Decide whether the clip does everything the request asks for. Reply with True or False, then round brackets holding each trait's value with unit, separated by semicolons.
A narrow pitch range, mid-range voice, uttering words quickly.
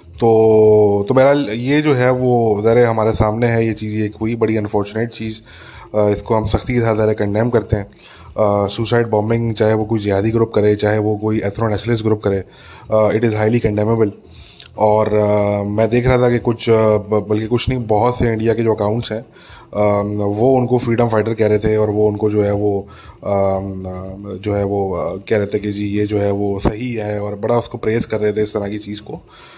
False (1.7 semitones; 110 Hz; 215 wpm)